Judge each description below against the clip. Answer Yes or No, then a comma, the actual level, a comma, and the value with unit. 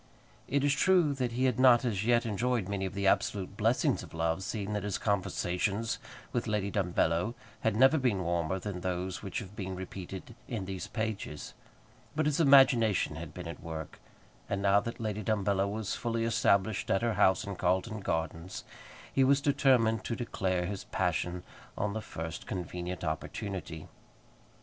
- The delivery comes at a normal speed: Yes, average, 170 wpm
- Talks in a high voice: No, low, 100 Hz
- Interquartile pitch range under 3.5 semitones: No, average, 4.1 semitones